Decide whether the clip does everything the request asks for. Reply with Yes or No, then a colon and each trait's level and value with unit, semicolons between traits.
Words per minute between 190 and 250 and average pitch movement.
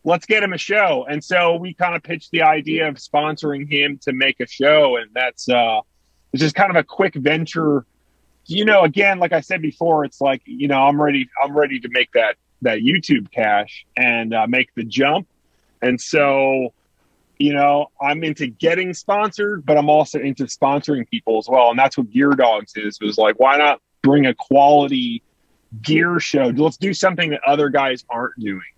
Yes: average, 200 wpm; average, 3.9 semitones